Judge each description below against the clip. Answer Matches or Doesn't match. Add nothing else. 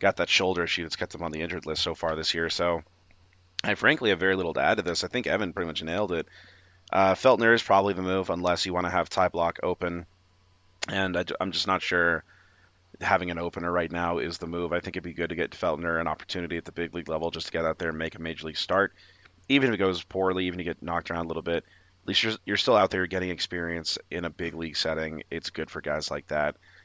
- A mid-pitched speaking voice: Doesn't match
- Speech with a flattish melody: Matches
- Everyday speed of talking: Doesn't match